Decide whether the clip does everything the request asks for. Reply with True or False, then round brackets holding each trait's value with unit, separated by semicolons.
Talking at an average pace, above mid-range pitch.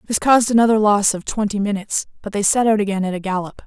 False (245 wpm; 205 Hz)